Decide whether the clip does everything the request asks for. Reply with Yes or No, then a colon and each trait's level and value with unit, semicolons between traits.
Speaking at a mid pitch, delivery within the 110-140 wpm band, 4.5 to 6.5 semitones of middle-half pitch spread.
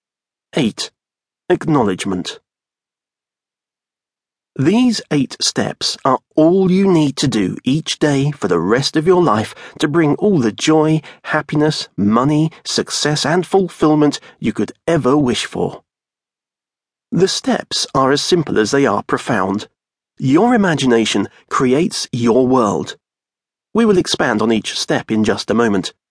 Yes: medium, 155 Hz; slow, 135 wpm; average, 5.2 semitones